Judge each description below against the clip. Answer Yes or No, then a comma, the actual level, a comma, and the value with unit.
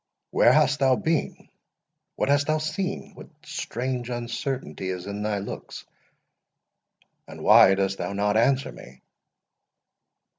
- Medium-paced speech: No, slow, 110 wpm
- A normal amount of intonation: No, wide, 6.1 semitones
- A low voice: Yes, low, 125 Hz